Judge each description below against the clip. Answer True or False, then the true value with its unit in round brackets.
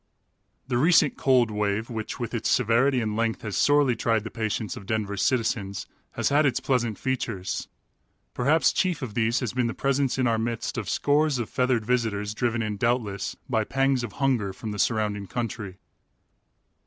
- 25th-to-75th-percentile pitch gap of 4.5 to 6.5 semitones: False (3.2 semitones)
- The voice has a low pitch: True (115 Hz)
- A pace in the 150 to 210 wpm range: True (180 wpm)